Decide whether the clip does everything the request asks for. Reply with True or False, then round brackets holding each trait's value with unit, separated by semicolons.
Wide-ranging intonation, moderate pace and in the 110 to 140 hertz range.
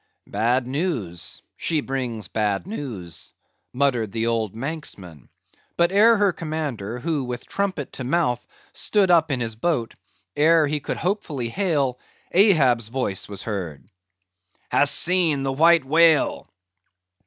False (6.4 semitones; 130 wpm; 135 Hz)